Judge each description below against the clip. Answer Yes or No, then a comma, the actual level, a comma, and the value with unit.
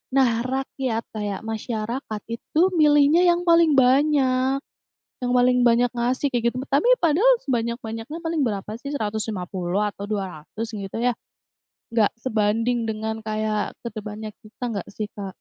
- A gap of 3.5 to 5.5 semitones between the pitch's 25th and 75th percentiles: Yes, average, 3.9 semitones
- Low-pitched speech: No, high, 230 Hz